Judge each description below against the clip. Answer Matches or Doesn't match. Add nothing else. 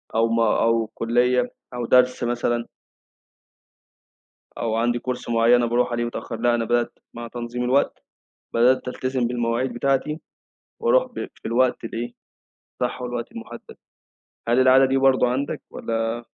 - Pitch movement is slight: Matches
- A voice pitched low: Matches